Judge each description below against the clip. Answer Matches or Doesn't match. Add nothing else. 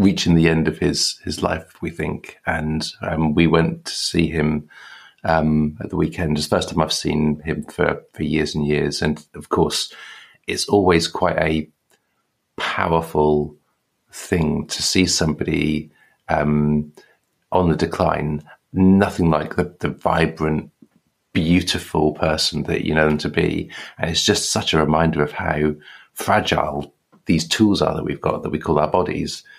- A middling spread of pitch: Doesn't match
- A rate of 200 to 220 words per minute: Doesn't match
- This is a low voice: Matches